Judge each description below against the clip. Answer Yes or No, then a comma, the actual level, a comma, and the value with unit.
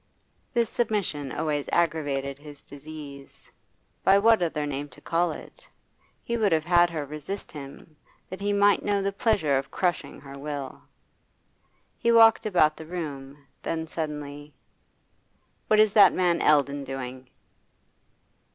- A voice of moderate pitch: Yes, medium, 155 Hz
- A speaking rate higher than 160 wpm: No, average, 140 wpm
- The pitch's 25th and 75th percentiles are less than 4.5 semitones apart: No, wide, 5.4 semitones